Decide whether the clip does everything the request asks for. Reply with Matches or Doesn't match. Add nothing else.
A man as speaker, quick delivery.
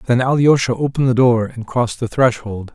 Doesn't match